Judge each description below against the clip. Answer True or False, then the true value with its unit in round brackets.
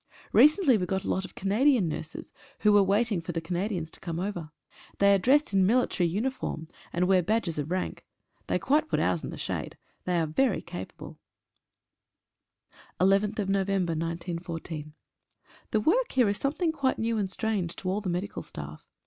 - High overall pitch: True (195 Hz)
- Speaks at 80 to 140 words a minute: False (170 wpm)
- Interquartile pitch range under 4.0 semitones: False (4.4 semitones)